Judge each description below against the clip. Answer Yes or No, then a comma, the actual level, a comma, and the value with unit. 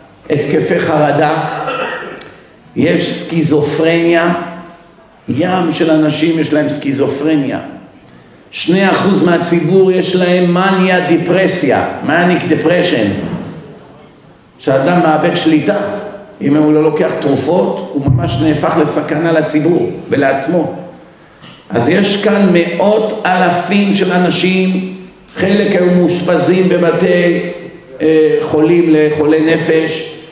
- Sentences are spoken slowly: Yes, slow, 95 wpm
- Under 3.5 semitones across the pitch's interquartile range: Yes, average, 2.8 semitones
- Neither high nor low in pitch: Yes, medium, 170 Hz